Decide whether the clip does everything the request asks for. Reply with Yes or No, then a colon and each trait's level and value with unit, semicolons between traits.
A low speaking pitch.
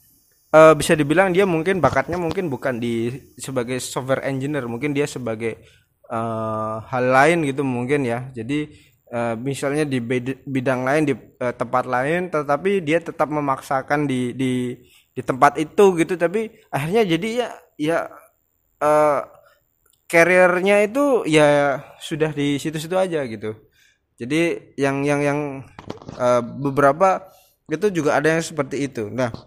No: medium, 145 Hz